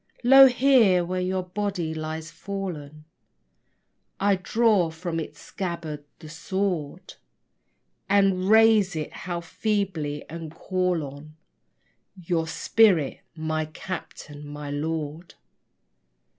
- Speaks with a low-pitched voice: No, medium, 175 Hz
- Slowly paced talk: Yes, slow, 105 wpm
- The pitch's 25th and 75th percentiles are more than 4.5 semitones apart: No, average, 3.8 semitones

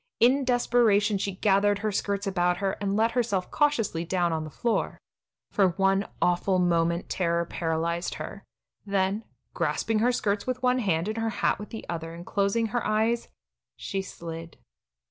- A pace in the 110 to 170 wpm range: Yes, average, 165 wpm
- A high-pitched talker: Yes, high, 200 Hz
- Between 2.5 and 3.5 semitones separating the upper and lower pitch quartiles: No, average, 4.2 semitones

